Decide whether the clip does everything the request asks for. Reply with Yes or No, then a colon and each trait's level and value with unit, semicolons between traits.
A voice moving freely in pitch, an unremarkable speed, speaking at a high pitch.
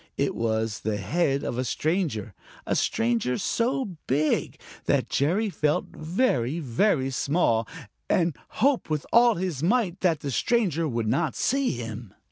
No: wide, 7.8 semitones; average, 145 wpm; medium, 150 Hz